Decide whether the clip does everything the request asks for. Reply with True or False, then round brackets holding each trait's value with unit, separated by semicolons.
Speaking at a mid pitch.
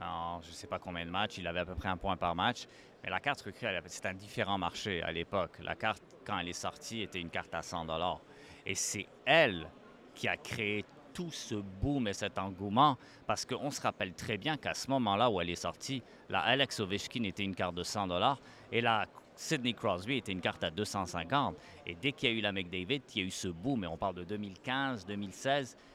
False (100 Hz)